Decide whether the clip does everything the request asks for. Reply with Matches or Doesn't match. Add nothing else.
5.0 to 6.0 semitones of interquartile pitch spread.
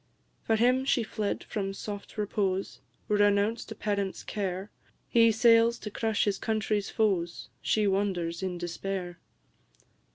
Doesn't match